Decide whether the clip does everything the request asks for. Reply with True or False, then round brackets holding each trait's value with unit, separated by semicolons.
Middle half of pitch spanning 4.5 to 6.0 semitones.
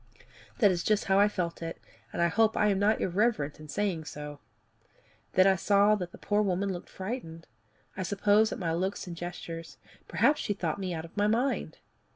False (3.6 semitones)